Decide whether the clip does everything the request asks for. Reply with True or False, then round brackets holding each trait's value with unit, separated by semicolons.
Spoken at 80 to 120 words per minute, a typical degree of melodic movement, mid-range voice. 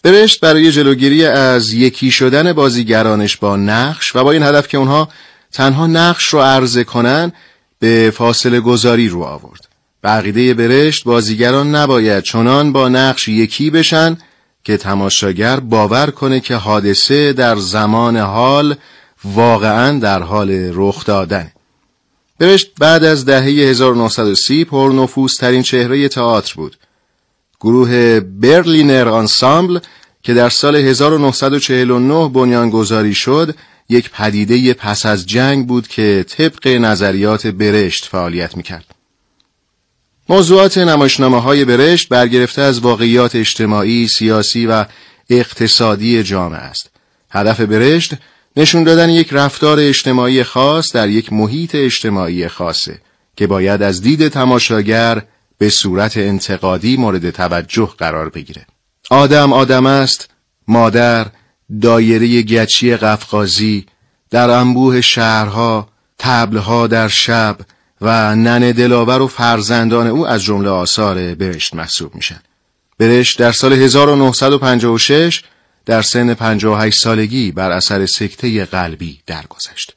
False (115 wpm; 4.1 semitones; 120 Hz)